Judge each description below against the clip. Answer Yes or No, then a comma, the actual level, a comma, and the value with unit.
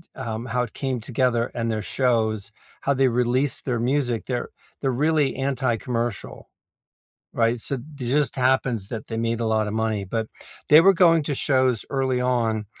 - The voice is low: Yes, low, 125 Hz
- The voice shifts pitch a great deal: No, average, 2.7 semitones